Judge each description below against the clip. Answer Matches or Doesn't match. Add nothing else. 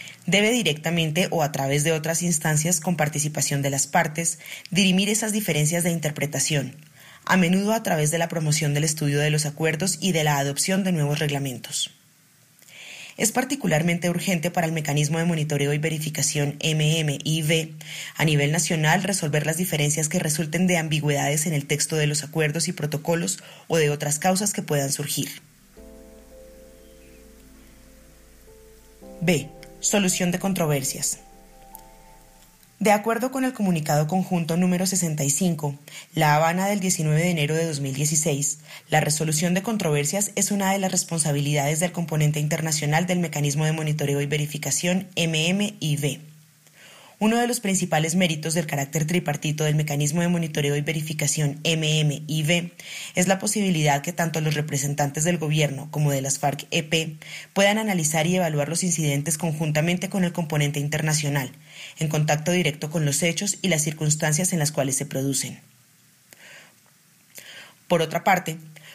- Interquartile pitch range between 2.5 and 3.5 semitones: Matches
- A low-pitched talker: Doesn't match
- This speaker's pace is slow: Doesn't match